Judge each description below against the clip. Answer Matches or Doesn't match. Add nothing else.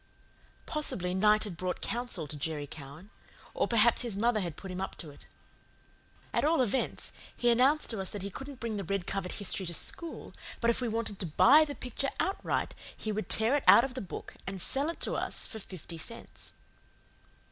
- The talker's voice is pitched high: Matches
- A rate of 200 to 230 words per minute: Matches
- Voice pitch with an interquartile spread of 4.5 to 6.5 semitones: Matches